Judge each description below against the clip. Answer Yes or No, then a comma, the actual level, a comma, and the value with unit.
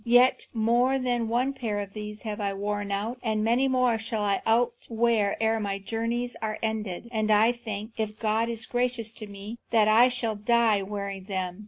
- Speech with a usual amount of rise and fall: No, narrow, 2.3 semitones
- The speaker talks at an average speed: Yes, average, 185 wpm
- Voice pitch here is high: Yes, high, 220 Hz